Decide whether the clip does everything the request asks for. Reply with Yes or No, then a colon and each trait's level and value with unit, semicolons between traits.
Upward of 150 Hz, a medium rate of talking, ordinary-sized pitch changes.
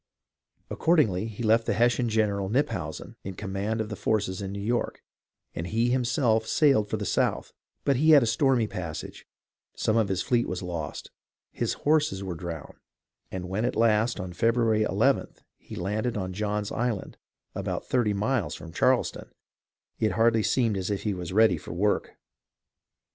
No: low, 110 Hz; average, 170 wpm; average, 3.6 semitones